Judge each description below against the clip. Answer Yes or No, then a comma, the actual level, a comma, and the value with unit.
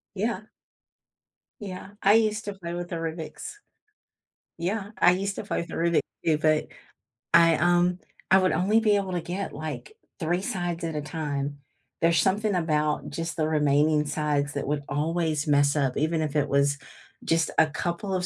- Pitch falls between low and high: Yes, medium, 165 Hz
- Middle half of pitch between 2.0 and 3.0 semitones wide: No, average, 3.5 semitones